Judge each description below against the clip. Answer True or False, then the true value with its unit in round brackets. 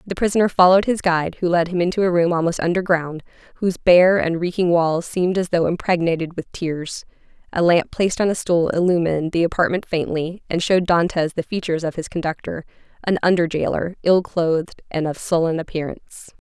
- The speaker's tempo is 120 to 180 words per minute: False (190 wpm)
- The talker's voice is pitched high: False (170 Hz)